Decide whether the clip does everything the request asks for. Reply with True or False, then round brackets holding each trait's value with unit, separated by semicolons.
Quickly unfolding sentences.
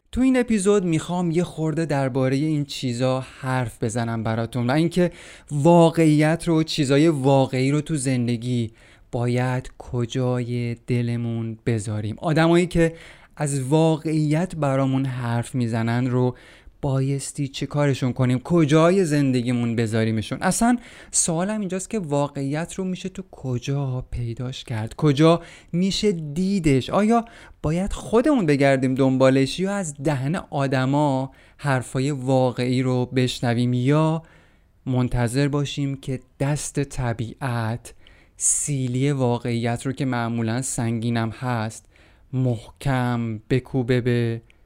False (110 wpm)